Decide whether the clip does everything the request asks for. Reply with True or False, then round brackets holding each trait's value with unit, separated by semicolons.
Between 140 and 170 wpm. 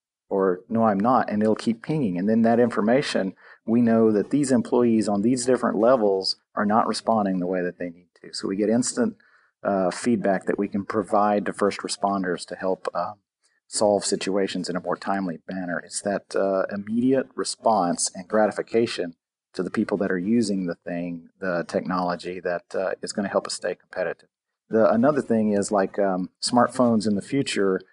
False (190 wpm)